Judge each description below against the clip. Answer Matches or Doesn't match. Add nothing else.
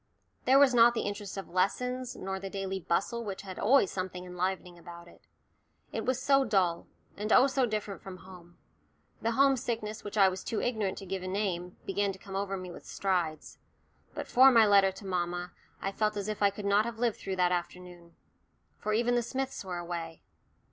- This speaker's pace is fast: Matches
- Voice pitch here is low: Doesn't match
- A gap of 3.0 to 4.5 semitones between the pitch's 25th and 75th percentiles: Matches